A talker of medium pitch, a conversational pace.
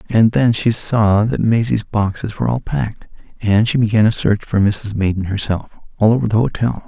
No: low, 110 Hz; average, 190 wpm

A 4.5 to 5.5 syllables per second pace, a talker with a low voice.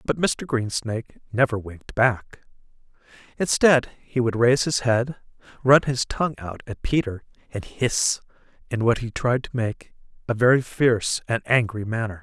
Yes: 4.8 syllables/s; low, 120 Hz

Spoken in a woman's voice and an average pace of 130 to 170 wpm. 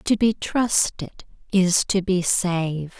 Yes: female; average, 140 wpm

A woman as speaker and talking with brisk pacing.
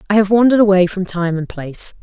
Yes: female; fast, 235 wpm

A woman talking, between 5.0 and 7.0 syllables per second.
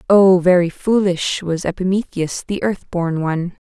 No: female; 4.6 syllables/s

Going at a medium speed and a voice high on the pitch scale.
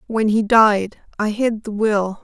Yes: average, 160 wpm; high, 215 Hz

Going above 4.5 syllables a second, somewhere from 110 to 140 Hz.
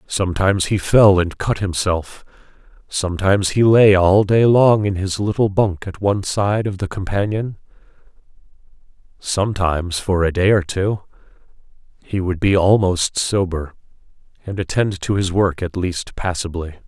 No: 4.7 syllables/s; very low, 95 Hz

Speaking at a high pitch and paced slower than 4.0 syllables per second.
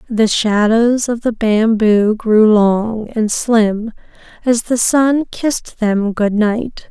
Yes: high, 220 Hz; 3.1 syllables/s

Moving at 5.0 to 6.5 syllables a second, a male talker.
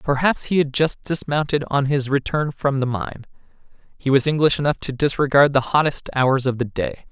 Yes: 5.2 syllables/s; male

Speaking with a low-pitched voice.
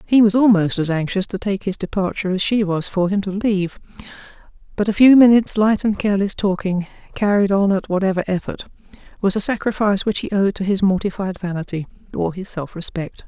No: high, 195 Hz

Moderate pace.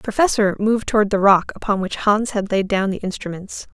No: fast, 220 wpm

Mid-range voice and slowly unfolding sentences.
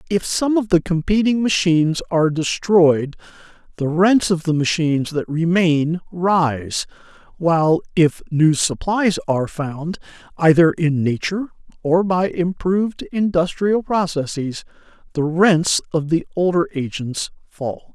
Yes: medium, 170 Hz; slow, 125 wpm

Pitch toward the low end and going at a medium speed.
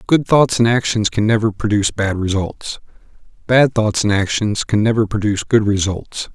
Yes: low, 110 Hz; average, 170 wpm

